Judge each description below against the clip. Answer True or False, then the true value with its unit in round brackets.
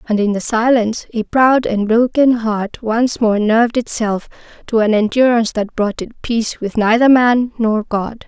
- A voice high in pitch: True (225 Hz)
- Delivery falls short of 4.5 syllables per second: False (4.6 syllables/s)